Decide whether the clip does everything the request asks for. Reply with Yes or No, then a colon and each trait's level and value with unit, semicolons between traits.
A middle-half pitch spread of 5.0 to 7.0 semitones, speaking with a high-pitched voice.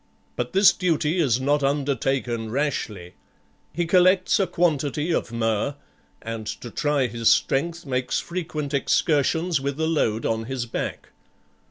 No: wide, 5.5 semitones; medium, 140 Hz